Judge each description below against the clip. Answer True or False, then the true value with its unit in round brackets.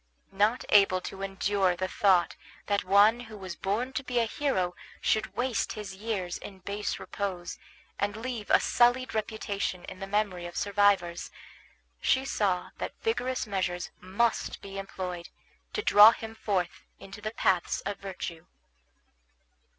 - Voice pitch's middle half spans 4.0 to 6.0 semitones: False (2.8 semitones)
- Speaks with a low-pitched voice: False (200 Hz)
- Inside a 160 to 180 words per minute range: False (150 wpm)